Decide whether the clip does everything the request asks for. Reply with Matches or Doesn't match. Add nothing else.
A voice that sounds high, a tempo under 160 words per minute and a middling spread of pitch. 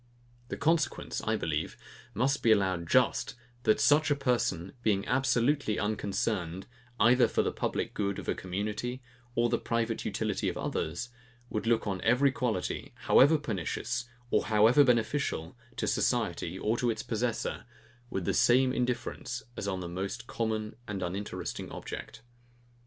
Doesn't match